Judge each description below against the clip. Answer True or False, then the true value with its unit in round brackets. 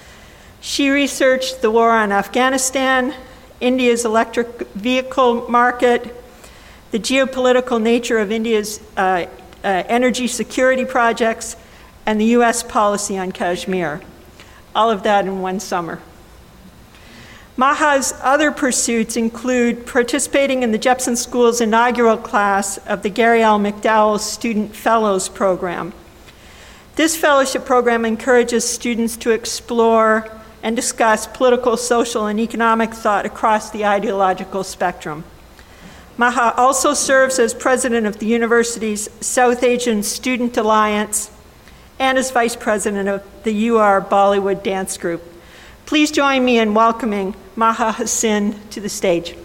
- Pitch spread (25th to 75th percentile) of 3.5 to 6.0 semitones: False (2.8 semitones)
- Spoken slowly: True (125 wpm)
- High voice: True (230 Hz)